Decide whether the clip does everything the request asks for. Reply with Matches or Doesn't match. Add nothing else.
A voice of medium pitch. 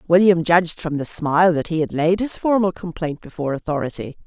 Matches